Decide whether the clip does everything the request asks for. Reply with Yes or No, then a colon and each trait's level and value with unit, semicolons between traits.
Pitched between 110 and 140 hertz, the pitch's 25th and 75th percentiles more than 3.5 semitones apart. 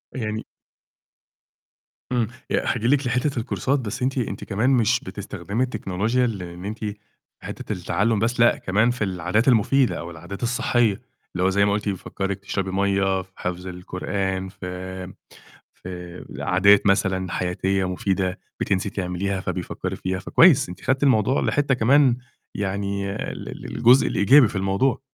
No: low, 100 Hz; average, 4.2 semitones